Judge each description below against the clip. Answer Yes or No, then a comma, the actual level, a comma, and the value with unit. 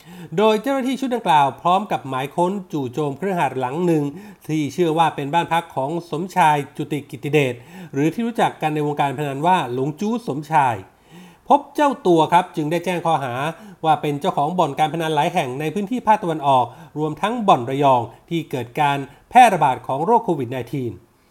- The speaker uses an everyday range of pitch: Yes, average, 4.2 semitones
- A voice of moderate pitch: Yes, medium, 160 Hz